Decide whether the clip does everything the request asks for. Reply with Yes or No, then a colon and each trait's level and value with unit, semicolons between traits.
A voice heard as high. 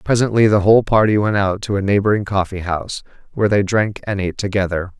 No: low, 100 Hz